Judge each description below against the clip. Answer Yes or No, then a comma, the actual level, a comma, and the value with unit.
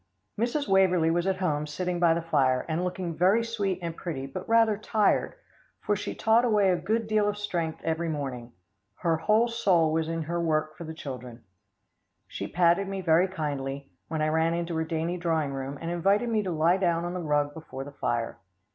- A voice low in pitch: No, medium, 170 Hz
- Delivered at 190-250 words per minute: Yes, fast, 205 wpm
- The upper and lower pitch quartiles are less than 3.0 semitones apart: No, average, 3.6 semitones